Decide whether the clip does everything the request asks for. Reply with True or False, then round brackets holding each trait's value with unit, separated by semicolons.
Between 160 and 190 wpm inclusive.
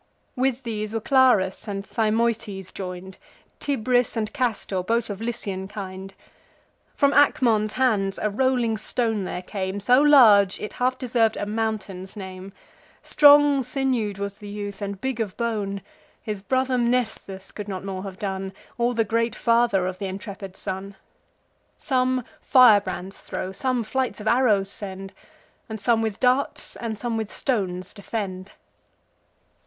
False (145 wpm)